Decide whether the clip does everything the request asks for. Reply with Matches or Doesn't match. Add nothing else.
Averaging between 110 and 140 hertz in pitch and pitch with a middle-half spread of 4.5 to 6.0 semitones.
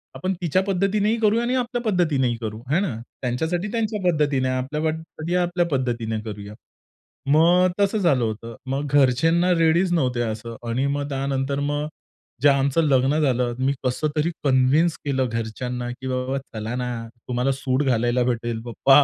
Matches